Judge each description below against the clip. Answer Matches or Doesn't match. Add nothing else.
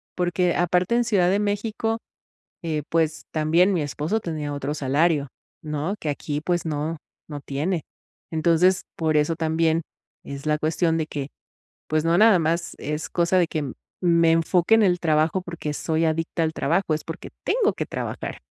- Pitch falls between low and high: Matches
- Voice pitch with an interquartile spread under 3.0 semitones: Matches